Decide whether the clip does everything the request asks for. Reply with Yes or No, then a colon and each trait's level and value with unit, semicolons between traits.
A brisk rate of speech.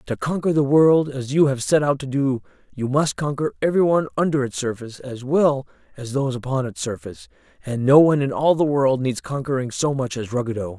Yes: fast, 210 wpm